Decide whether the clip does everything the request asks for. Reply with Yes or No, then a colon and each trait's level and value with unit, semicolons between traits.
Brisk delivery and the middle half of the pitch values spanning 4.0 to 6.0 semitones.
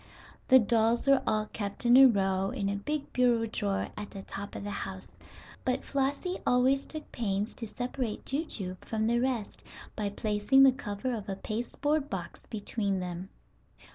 No: average, 170 wpm; average, 4.4 semitones